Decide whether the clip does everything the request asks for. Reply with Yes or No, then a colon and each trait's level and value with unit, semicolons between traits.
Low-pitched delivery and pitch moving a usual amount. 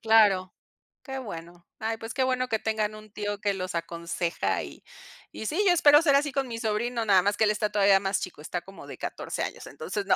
No: high, 210 Hz; average, 3.4 semitones